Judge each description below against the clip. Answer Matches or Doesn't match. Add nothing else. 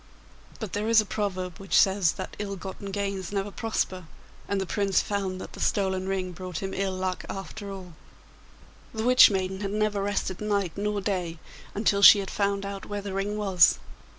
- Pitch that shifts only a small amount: Matches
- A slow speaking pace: Doesn't match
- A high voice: Matches